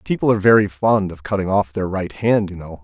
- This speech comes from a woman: No, male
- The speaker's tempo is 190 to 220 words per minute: No, fast, 255 wpm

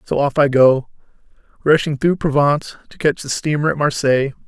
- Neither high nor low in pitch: Yes, medium, 145 Hz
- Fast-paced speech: No, average, 175 wpm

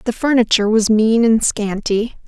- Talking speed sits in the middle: Yes, average, 160 wpm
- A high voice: Yes, high, 220 Hz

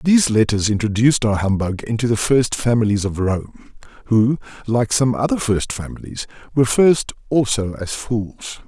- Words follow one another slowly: No, average, 150 wpm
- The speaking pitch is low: Yes, low, 115 Hz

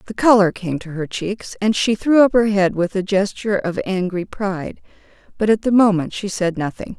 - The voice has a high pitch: Yes, high, 200 Hz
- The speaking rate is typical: No, fast, 215 wpm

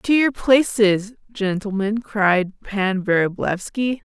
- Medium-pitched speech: No, high, 210 Hz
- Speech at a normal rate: No, slow, 100 wpm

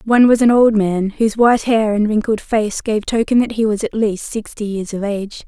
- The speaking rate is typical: No, fast, 240 wpm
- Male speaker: No, female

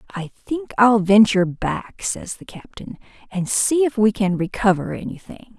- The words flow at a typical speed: Yes, average, 160 wpm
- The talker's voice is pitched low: No, high, 210 Hz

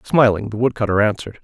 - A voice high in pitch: No, low, 110 Hz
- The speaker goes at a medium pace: Yes, average, 170 wpm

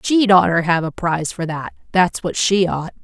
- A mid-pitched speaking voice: Yes, medium, 175 Hz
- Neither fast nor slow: No, fast, 215 wpm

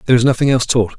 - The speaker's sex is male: Yes, male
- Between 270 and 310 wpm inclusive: Yes, fast, 305 wpm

